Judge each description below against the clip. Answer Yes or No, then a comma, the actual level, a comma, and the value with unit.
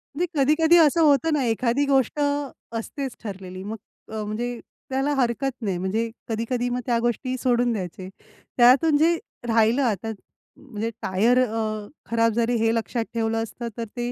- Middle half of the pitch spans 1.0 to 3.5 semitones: Yes, average, 3.0 semitones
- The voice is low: No, high, 235 Hz